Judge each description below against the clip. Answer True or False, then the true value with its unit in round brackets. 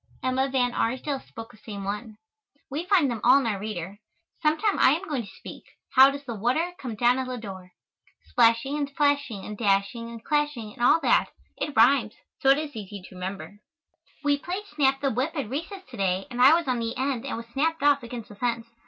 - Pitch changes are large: False (4.6 semitones)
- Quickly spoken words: True (215 wpm)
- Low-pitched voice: False (250 Hz)